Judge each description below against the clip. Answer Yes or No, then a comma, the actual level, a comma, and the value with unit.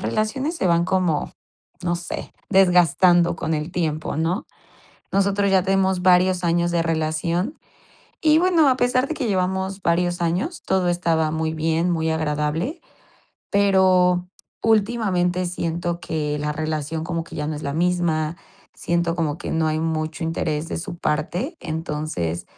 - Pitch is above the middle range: No, medium, 175 Hz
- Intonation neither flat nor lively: Yes, average, 3.0 semitones